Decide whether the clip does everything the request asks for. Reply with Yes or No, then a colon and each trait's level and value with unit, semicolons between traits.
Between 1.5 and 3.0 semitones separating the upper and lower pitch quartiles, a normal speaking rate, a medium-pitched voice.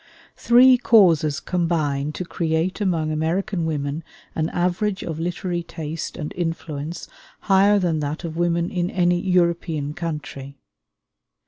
No: narrow, 2.5 semitones; slow, 125 wpm; medium, 170 Hz